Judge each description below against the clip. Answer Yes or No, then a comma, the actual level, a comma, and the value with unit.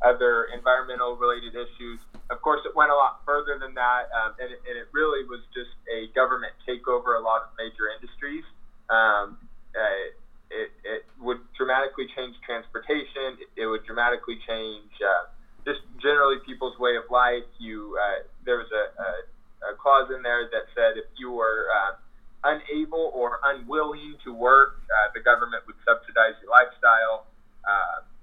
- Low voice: Yes, low, 125 Hz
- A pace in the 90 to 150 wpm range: No, average, 165 wpm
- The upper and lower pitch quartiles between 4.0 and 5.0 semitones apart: No, average, 3.5 semitones